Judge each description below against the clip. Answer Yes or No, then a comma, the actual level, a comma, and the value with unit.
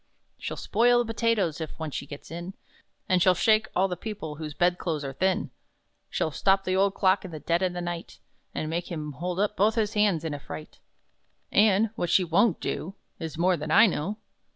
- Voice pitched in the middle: Yes, medium, 180 Hz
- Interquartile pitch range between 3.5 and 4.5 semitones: Yes, average, 4.0 semitones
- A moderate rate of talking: No, fast, 215 wpm